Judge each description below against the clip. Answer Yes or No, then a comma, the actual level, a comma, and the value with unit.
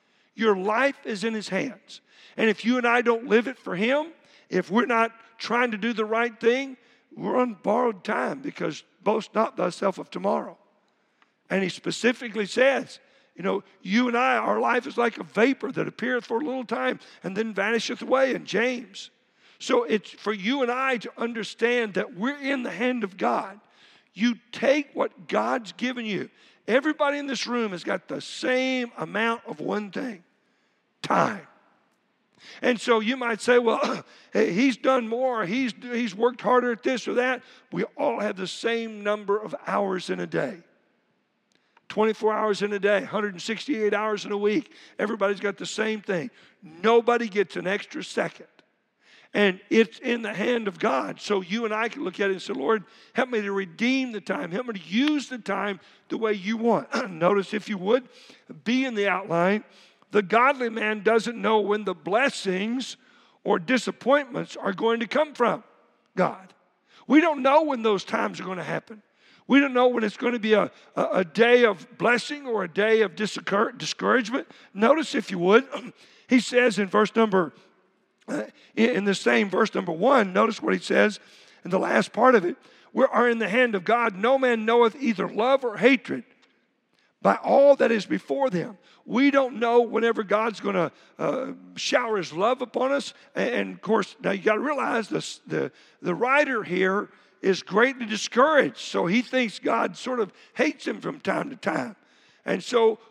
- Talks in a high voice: Yes, high, 230 Hz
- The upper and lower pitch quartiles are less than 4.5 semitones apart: Yes, average, 3.4 semitones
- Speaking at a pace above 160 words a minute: Yes, average, 185 wpm